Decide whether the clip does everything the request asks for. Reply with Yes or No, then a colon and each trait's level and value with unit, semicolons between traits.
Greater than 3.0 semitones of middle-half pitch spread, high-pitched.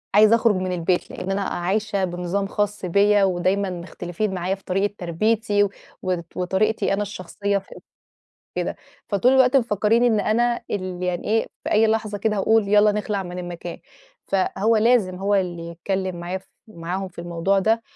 No: average, 2.7 semitones; high, 195 Hz